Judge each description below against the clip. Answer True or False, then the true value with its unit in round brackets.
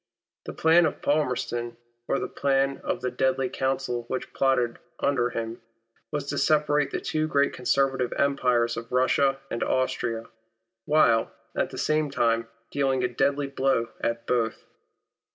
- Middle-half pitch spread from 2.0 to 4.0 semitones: True (2.9 semitones)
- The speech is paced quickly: False (155 wpm)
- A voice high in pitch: False (130 Hz)